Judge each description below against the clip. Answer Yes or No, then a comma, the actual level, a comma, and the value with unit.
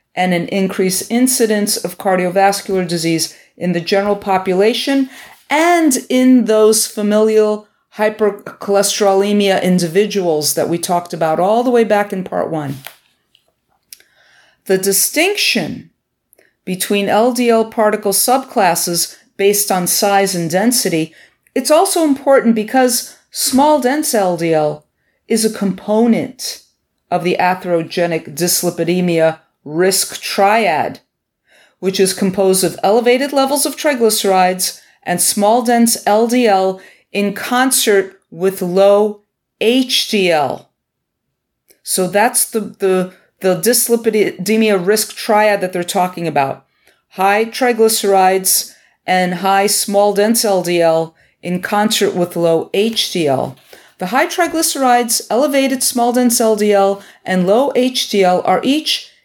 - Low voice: No, high, 205 Hz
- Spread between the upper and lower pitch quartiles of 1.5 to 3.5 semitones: No, average, 4.2 semitones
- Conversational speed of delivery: No, slow, 110 wpm